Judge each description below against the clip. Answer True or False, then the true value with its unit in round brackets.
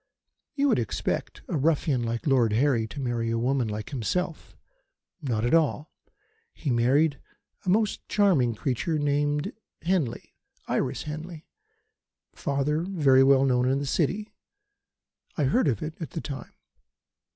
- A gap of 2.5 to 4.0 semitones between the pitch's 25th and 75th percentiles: False (4.4 semitones)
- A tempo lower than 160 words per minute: True (140 wpm)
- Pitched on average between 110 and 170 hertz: True (140 Hz)